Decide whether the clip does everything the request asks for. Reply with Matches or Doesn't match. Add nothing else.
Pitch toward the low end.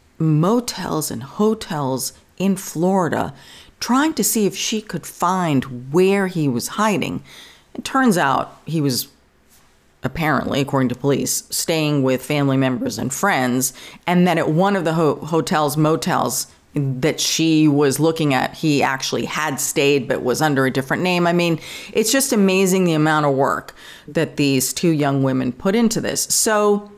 Doesn't match